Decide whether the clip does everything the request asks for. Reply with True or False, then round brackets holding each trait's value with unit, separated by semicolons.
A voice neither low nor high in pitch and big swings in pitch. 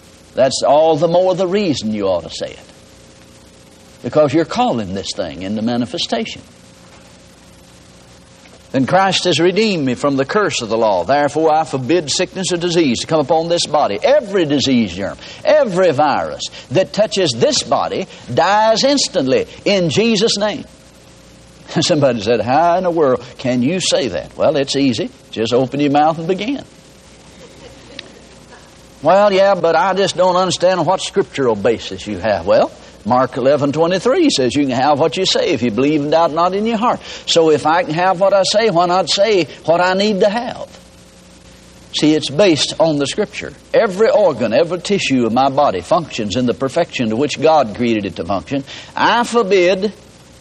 True (165 Hz; 7.2 semitones)